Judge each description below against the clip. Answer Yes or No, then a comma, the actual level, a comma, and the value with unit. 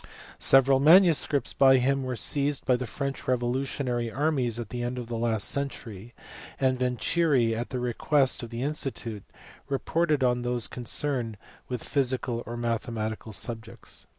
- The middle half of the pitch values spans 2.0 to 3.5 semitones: Yes, average, 2.7 semitones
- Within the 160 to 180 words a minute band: No, average, 150 wpm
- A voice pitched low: Yes, low, 125 Hz